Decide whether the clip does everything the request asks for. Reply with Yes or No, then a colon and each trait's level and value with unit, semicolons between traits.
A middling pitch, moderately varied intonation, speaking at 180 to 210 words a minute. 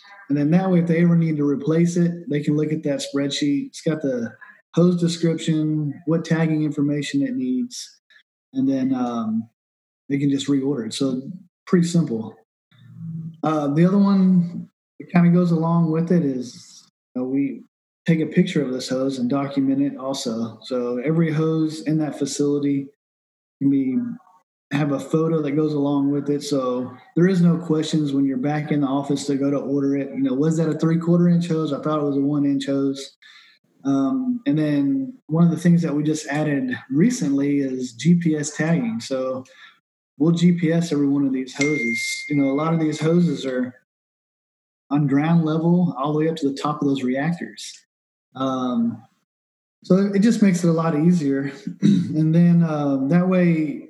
Yes: medium, 150 Hz; average, 3.6 semitones; average, 190 wpm